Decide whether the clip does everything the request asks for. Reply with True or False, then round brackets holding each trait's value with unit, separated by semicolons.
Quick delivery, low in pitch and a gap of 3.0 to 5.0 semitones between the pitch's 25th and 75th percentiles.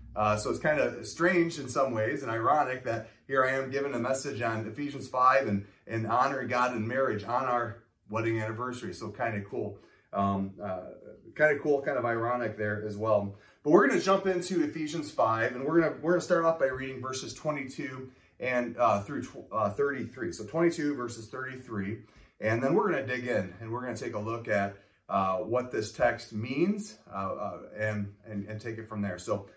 True (215 wpm; 120 Hz; 4.4 semitones)